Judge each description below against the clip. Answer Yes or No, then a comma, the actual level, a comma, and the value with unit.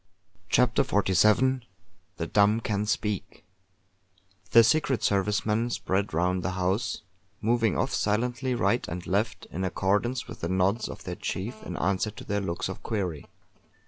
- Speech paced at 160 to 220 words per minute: No, average, 150 wpm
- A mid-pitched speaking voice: No, low, 105 Hz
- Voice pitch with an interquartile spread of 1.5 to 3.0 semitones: No, average, 3.7 semitones